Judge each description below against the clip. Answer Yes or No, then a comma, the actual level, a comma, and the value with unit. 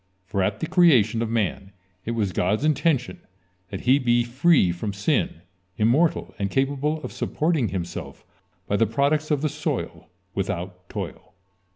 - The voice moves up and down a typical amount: No, wide, 7.0 semitones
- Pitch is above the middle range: No, low, 115 Hz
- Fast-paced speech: No, average, 155 wpm